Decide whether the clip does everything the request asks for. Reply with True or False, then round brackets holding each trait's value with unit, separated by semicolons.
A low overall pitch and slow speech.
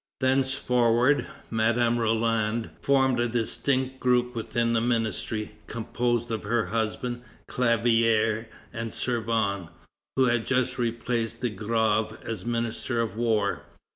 True (115 Hz; 115 wpm)